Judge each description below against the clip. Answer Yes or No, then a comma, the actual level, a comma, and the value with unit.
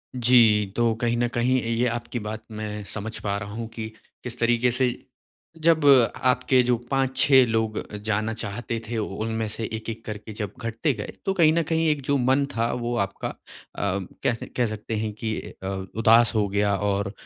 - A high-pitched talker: No, low, 115 Hz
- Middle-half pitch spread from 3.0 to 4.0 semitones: No, narrow, 2.6 semitones